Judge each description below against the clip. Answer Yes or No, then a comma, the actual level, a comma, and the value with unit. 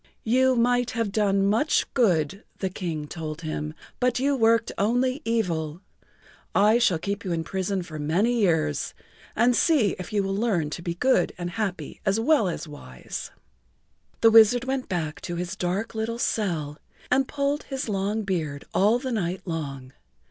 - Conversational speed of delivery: Yes, average, 170 wpm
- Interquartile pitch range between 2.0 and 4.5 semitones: No, wide, 5.5 semitones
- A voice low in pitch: No, high, 200 Hz